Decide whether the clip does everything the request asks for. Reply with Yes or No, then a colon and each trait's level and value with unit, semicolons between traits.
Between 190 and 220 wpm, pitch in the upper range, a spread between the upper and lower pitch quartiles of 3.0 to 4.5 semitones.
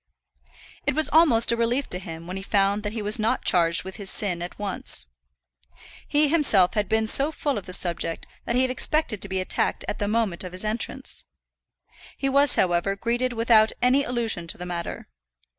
No: average, 200 wpm; high, 215 Hz; average, 5.0 semitones